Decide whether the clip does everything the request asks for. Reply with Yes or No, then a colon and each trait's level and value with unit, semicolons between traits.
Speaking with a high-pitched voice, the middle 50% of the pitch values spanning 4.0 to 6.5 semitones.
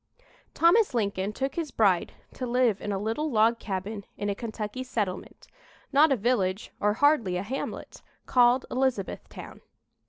Yes: high, 225 Hz; average, 4.3 semitones